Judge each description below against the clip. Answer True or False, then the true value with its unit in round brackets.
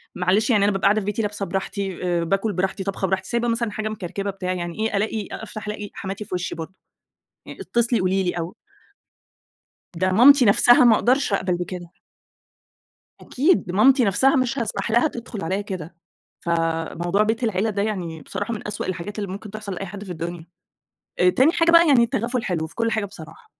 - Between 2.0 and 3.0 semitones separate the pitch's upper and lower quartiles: False (3.5 semitones)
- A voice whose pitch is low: False (200 Hz)